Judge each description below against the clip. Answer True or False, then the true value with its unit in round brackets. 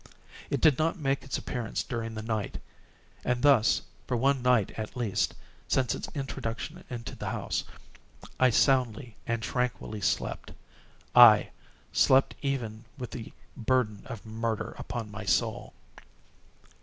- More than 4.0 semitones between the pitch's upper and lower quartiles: False (3.0 semitones)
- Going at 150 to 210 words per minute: False (135 wpm)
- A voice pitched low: True (120 Hz)